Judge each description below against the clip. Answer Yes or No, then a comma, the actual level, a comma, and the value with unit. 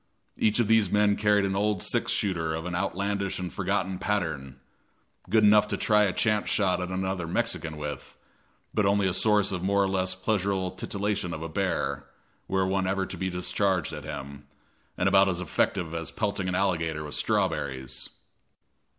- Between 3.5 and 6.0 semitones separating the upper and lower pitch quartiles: No, average, 2.8 semitones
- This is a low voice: Yes, very low, 95 Hz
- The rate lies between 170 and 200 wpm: Yes, average, 180 wpm